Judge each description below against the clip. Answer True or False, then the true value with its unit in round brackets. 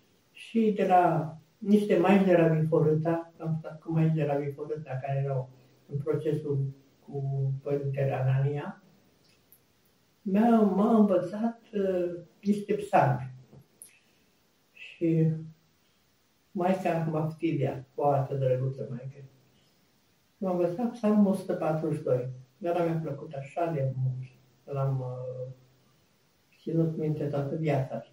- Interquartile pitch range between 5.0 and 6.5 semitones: False (4.3 semitones)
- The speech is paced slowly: True (110 wpm)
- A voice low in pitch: False (155 Hz)